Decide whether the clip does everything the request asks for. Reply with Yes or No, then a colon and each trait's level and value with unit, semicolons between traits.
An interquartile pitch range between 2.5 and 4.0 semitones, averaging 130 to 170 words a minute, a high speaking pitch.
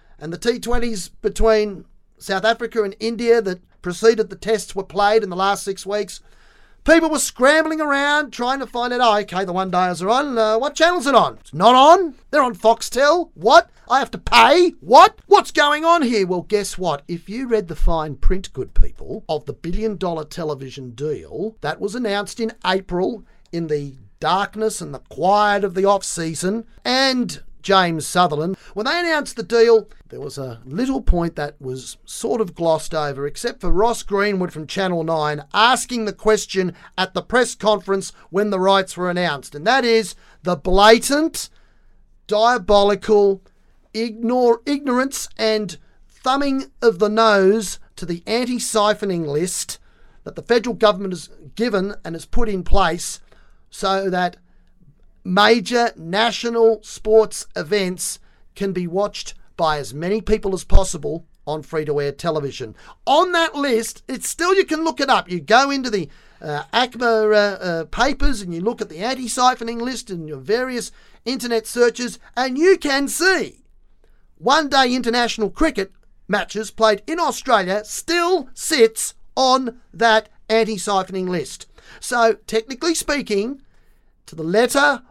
No: average, 5.0 semitones; average, 155 wpm; high, 215 Hz